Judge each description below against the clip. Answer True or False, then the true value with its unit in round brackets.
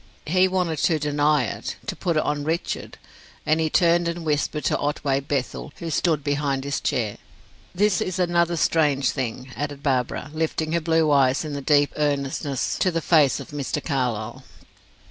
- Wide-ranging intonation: False (2.9 semitones)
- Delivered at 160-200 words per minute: True (175 wpm)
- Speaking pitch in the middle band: True (150 Hz)